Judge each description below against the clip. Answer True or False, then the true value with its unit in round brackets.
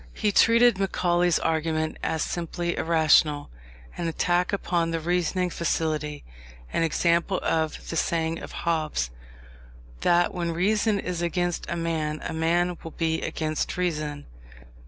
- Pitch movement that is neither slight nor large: False (1.8 semitones)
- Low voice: False (170 Hz)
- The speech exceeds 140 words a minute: False (135 wpm)